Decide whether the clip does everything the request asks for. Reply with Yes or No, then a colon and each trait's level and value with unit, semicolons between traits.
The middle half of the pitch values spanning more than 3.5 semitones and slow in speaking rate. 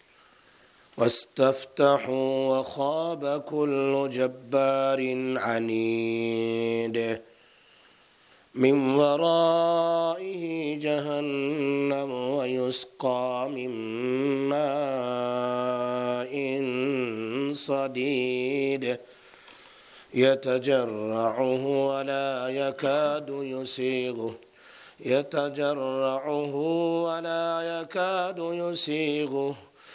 No: narrow, 2.5 semitones; slow, 40 wpm